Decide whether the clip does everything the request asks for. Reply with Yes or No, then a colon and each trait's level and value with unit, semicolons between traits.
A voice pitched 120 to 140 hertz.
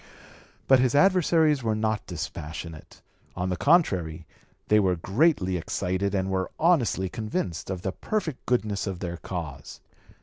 No: very low, 95 Hz